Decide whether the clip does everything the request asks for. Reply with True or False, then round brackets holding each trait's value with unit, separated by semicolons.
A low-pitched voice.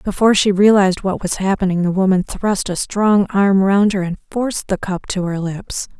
False (195 Hz)